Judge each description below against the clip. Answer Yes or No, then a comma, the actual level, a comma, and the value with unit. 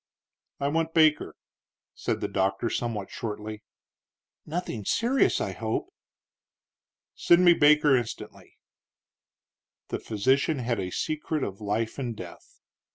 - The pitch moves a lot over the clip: Yes, wide, 6.7 semitones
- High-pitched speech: No, low, 125 Hz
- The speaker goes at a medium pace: No, slow, 115 wpm